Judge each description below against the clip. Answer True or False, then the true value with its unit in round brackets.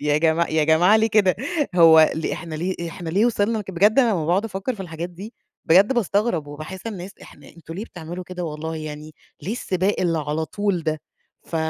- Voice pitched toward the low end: False (175 Hz)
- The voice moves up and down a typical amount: True (4.1 semitones)